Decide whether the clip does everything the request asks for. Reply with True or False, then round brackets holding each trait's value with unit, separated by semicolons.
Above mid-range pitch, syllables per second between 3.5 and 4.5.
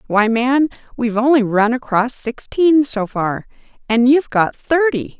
True (245 Hz; 4.4 syllables/s)